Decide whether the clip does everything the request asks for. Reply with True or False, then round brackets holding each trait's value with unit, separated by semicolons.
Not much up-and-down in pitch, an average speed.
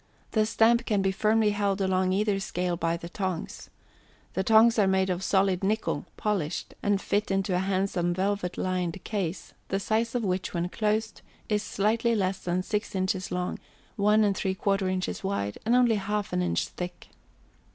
True (2.3 semitones; 170 wpm)